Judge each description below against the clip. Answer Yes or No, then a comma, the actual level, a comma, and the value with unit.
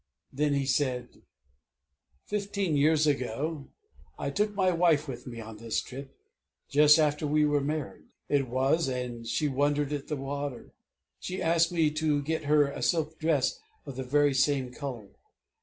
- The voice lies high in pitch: No, medium, 145 Hz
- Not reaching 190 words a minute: Yes, average, 160 wpm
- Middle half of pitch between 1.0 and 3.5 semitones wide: Yes, average, 2.8 semitones